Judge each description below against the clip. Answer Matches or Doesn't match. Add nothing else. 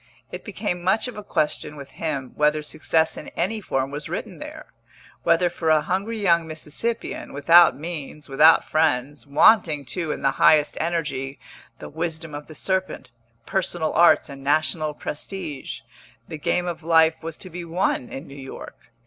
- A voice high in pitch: Doesn't match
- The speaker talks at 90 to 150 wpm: Doesn't match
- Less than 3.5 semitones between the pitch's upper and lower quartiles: Matches